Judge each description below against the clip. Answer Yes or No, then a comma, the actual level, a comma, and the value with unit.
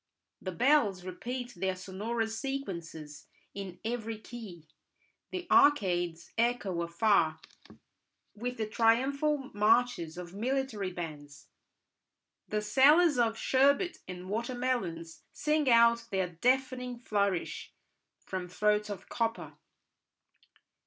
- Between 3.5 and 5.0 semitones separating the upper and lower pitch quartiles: No, wide, 5.5 semitones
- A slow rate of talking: Yes, slow, 105 wpm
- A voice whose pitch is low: No, high, 220 Hz